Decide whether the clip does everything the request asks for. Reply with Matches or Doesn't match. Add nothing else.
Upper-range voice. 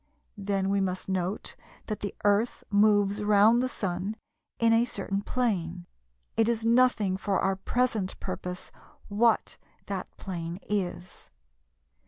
Matches